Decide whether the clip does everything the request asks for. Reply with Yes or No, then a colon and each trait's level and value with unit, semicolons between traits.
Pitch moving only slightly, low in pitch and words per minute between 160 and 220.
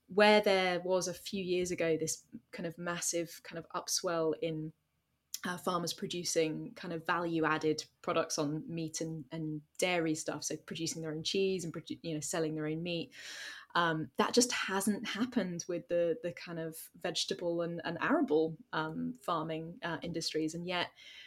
No: narrow, 2.1 semitones; medium, 170 Hz; average, 170 wpm